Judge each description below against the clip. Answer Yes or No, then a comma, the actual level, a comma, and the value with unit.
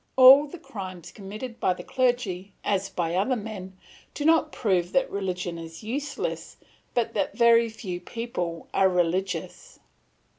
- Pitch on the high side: Yes, high, 200 Hz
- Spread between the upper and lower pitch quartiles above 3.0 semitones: Yes, average, 5.3 semitones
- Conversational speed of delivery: Yes, average, 145 wpm